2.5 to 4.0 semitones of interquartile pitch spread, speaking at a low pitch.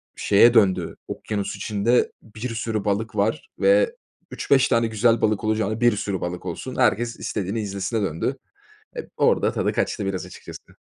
Yes: average, 2.8 semitones; low, 110 Hz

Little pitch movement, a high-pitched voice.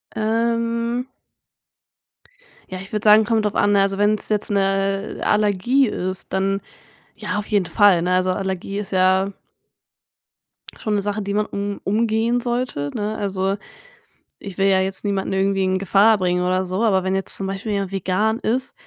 Yes: narrow, 2.1 semitones; high, 200 Hz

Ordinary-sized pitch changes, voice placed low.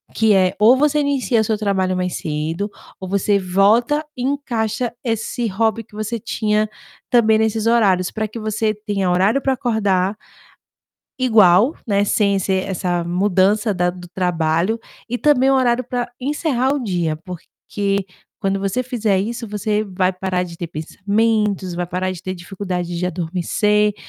No: average, 3.7 semitones; high, 205 Hz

